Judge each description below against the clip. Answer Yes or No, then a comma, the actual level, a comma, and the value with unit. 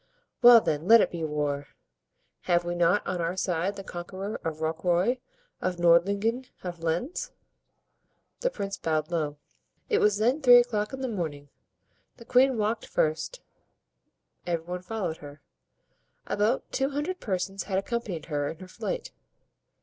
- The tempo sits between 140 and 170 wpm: Yes, average, 150 wpm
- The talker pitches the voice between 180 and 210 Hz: Yes, medium, 185 Hz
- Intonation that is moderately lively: No, wide, 5.8 semitones